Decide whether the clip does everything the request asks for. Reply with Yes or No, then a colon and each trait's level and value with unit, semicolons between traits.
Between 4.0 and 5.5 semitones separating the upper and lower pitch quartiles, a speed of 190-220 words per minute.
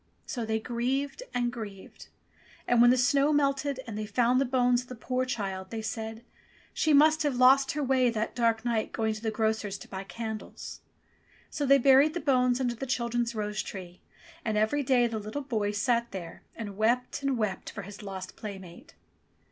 No: average, 3.3 semitones; average, 195 wpm